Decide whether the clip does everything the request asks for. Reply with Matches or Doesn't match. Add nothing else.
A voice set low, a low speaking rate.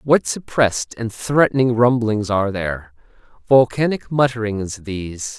Matches